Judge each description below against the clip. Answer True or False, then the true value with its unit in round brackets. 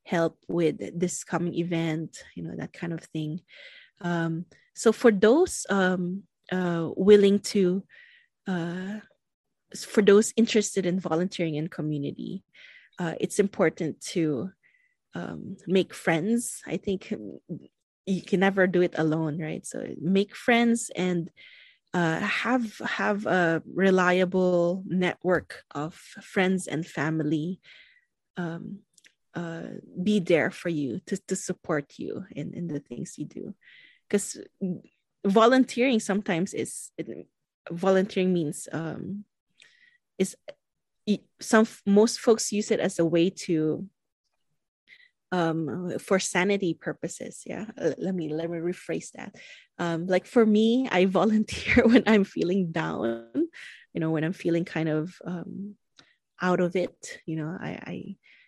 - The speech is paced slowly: True (130 wpm)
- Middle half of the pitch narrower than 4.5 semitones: True (4.0 semitones)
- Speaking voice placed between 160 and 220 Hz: True (185 Hz)